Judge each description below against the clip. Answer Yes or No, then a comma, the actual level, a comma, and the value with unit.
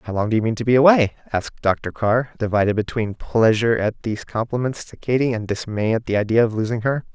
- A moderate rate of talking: No, fast, 225 wpm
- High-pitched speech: No, low, 115 Hz